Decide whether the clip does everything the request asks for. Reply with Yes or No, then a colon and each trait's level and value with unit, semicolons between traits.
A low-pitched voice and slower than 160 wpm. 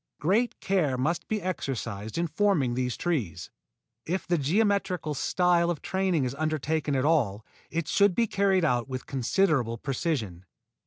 No: medium, 155 Hz; average, 150 wpm